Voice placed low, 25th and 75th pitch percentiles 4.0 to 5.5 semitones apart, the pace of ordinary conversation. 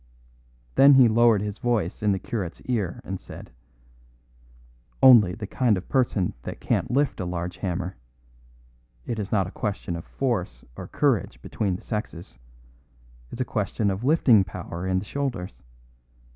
Yes: low, 105 Hz; average, 4.5 semitones; average, 160 wpm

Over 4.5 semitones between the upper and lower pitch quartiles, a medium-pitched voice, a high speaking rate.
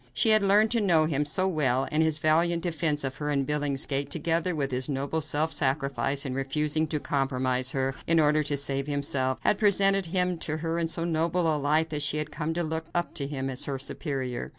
No: average, 3.1 semitones; medium, 150 Hz; fast, 220 wpm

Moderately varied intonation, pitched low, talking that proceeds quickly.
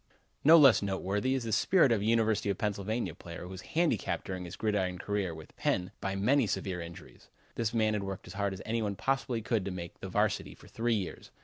Yes: average, 3.4 semitones; low, 105 Hz; fast, 225 wpm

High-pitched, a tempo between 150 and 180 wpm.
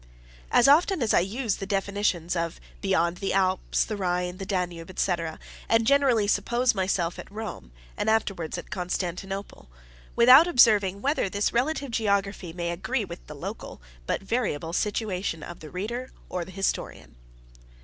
Yes: high, 195 Hz; average, 155 wpm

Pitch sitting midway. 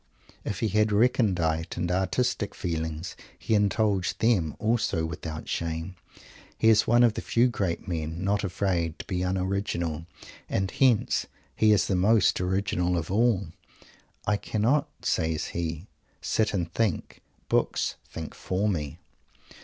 No: very low, 95 Hz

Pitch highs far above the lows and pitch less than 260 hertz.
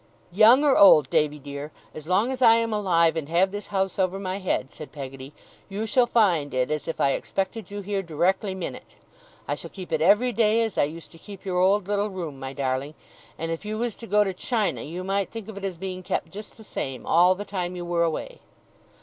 No: average, 4.2 semitones; medium, 185 Hz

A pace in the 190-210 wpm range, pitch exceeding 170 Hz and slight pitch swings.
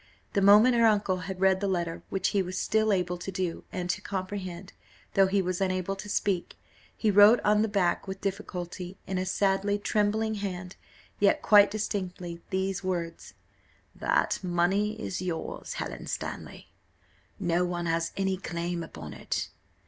No: average, 165 wpm; high, 190 Hz; narrow, 2.3 semitones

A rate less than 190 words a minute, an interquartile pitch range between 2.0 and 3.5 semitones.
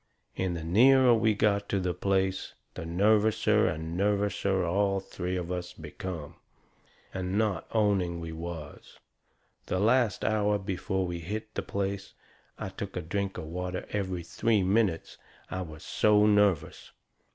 Yes: average, 150 wpm; average, 2.8 semitones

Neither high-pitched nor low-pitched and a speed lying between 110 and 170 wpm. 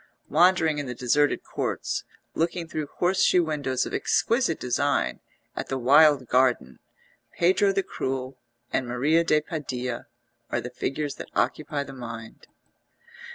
Yes: medium, 145 Hz; slow, 135 wpm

